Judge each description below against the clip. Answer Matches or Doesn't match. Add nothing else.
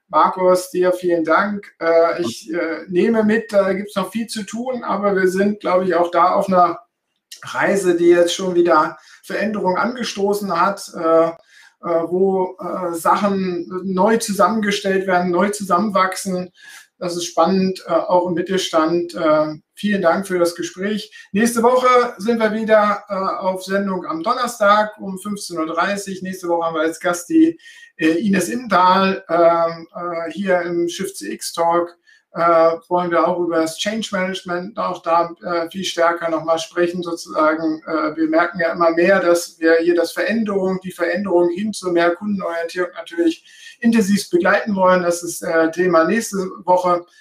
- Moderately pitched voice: Matches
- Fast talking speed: Doesn't match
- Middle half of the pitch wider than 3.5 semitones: Doesn't match